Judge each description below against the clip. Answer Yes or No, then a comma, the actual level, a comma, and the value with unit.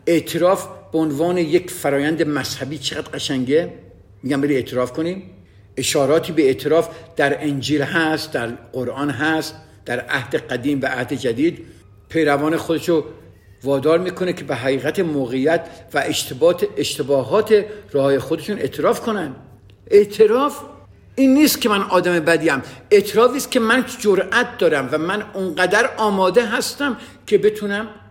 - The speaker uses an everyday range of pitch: No, wide, 6.5 semitones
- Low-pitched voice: No, medium, 160 Hz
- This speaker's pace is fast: No, average, 135 wpm